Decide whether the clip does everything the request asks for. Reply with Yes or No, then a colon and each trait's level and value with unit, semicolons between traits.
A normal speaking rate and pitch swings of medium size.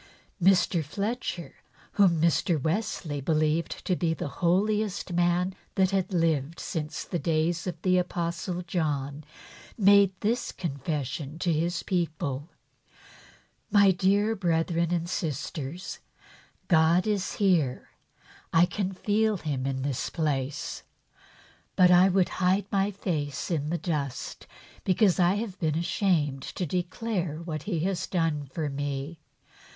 No: slow, 130 wpm; average, 3.6 semitones